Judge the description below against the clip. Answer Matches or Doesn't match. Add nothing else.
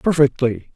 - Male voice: Matches